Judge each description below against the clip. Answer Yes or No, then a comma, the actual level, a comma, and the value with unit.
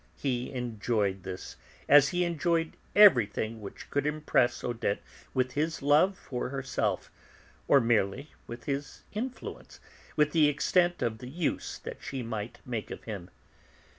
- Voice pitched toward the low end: Yes, low, 130 Hz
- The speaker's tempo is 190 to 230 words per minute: No, average, 140 wpm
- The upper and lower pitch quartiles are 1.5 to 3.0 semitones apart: No, average, 4.8 semitones